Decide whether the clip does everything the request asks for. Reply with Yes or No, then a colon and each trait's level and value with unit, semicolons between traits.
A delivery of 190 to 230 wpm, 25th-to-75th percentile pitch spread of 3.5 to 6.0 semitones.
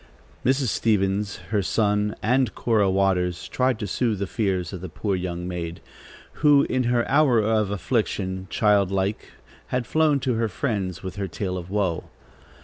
No: average, 160 wpm; average, 3.9 semitones